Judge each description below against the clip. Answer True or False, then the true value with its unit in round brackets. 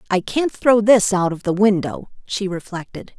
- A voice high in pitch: True (200 Hz)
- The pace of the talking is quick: False (190 wpm)